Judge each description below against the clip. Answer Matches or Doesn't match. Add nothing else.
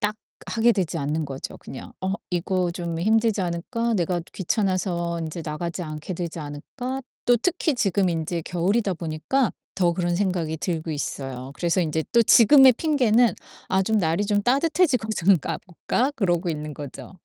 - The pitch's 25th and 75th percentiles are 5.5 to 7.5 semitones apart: Doesn't match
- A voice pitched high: Doesn't match